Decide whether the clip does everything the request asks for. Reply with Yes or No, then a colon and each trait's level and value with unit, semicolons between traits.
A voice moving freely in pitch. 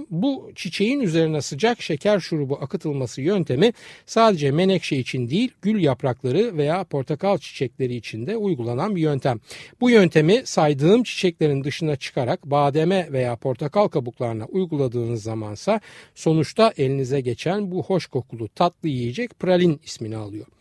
Yes: wide, 6.3 semitones